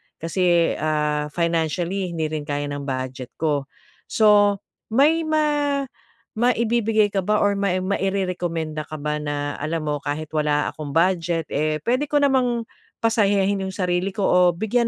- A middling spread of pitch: No, wide, 5.9 semitones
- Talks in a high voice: No, medium, 180 Hz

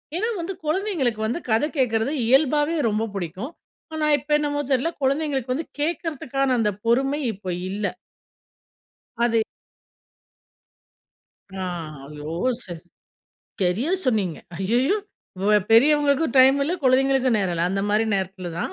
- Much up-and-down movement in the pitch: Yes, wide, 5.9 semitones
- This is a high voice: Yes, very high, 255 Hz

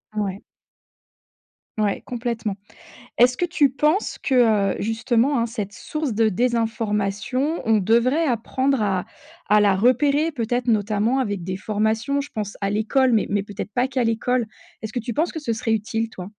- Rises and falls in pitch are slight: No, average, 3.6 semitones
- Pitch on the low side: No, high, 230 Hz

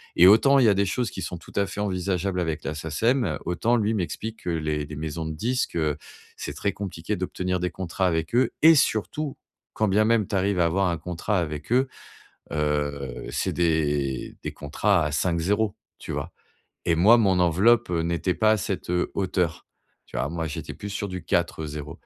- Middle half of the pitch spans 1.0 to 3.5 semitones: No, average, 4.3 semitones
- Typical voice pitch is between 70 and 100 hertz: Yes, very low, 90 Hz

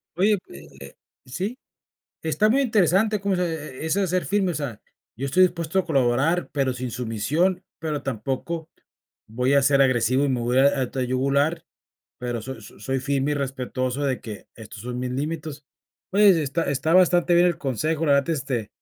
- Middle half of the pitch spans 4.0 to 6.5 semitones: Yes, average, 5.1 semitones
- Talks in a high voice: No, medium, 140 Hz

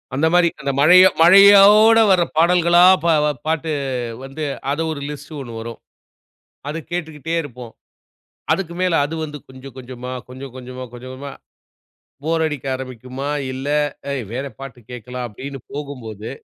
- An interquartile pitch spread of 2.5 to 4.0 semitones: No, average, 4.5 semitones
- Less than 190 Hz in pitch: Yes, medium, 140 Hz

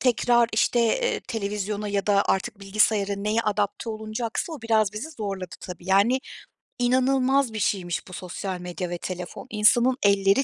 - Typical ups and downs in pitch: Yes, average, 3.3 semitones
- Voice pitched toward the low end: No, high, 210 Hz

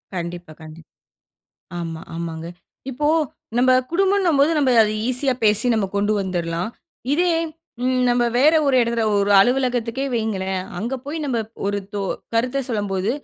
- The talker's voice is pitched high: Yes, high, 230 Hz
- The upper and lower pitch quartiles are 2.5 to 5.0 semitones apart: No, wide, 5.6 semitones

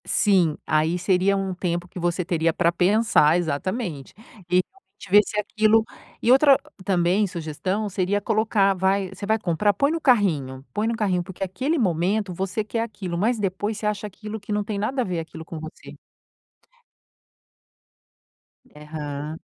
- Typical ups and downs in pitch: Yes, average, 3.6 semitones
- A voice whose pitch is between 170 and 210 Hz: Yes, high, 190 Hz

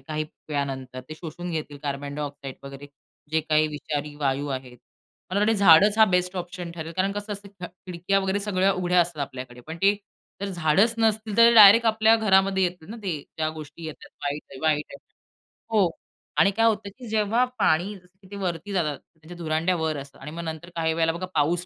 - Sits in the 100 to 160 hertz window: No, medium, 175 Hz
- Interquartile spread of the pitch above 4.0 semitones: Yes, average, 4.6 semitones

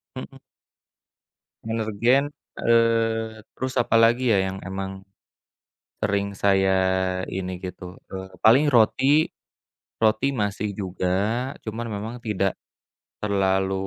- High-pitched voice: No, low, 105 Hz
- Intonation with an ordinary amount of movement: Yes, average, 3.2 semitones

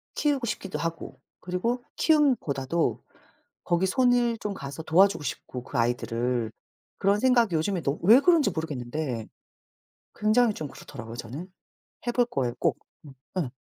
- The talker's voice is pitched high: No, medium, 170 Hz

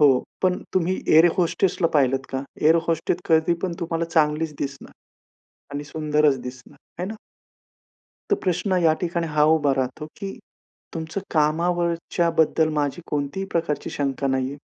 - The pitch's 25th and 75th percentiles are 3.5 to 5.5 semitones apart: No, average, 3.0 semitones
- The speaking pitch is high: No, medium, 160 Hz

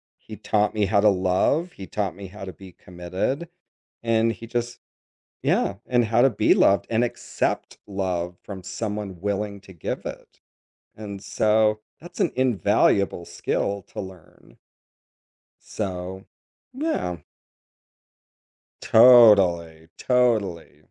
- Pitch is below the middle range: Yes, low, 100 Hz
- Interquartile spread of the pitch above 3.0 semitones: Yes, average, 3.4 semitones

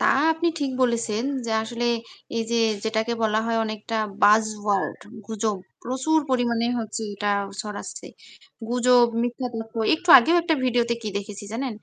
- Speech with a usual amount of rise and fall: No, narrow, 2.3 semitones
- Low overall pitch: No, high, 230 Hz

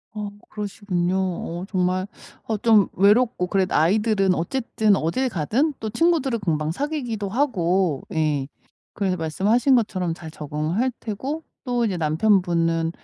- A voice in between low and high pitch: No, high, 195 Hz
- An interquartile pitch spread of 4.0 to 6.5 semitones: Yes, average, 5.2 semitones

